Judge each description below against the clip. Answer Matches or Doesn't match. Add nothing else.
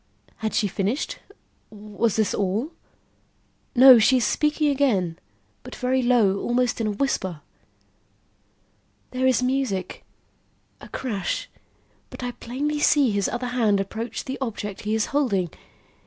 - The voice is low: Doesn't match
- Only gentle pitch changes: Doesn't match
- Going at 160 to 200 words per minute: Doesn't match